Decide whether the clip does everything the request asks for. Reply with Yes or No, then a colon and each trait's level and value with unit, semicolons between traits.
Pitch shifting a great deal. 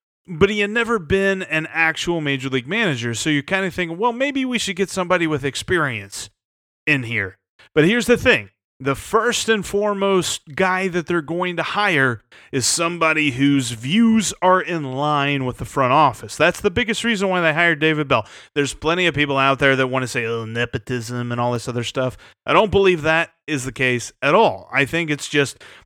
Yes: wide, 6.1 semitones